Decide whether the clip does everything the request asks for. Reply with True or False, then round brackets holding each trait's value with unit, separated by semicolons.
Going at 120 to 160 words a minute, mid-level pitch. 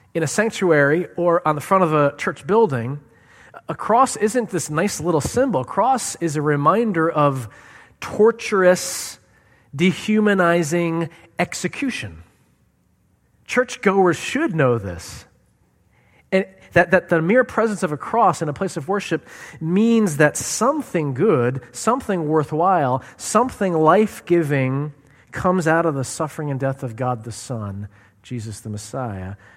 True (140 wpm; 160 Hz)